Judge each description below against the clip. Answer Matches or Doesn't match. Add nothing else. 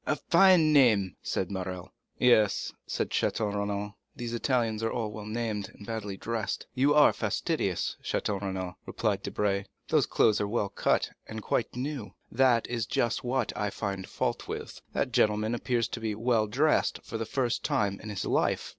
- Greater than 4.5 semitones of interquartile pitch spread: Doesn't match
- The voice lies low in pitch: Matches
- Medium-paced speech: Matches